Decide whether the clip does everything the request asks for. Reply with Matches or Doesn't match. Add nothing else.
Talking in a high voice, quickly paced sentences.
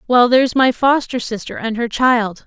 Doesn't match